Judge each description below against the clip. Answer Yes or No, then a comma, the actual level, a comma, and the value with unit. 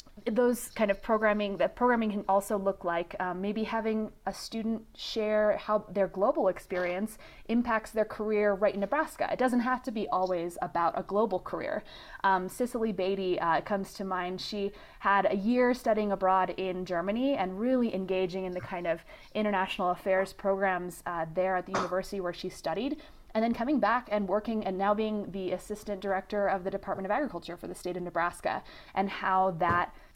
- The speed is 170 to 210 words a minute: Yes, average, 185 wpm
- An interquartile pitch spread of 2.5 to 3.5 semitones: Yes, average, 2.8 semitones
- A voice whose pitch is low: No, high, 200 Hz